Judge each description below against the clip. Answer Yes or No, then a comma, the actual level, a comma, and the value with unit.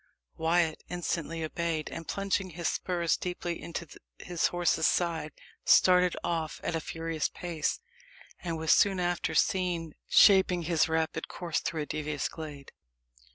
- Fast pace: No, average, 140 wpm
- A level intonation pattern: Yes, narrow, 1.7 semitones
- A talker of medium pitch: Yes, medium, 170 Hz